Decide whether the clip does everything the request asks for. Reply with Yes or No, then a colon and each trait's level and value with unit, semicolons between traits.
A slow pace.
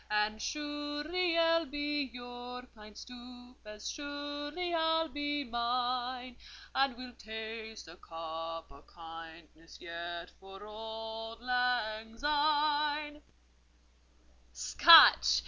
Yes: slow, 95 wpm